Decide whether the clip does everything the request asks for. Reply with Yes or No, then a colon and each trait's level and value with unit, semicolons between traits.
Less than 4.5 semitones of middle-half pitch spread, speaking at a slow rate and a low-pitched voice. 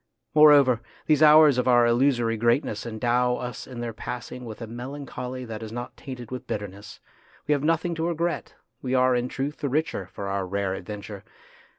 No: average, 4.0 semitones; average, 195 wpm; low, 125 Hz